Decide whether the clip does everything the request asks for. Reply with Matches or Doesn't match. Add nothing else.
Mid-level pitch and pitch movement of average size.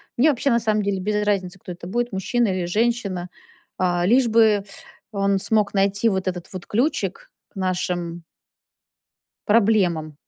Doesn't match